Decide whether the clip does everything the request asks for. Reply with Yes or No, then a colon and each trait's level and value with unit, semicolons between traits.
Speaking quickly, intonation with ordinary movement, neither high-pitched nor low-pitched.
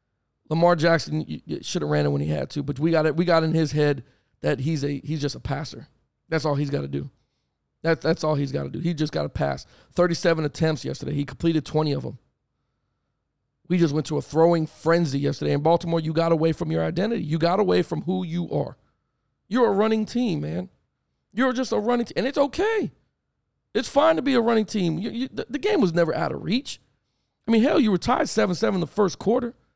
No: fast, 230 wpm; wide, 6.3 semitones; medium, 165 Hz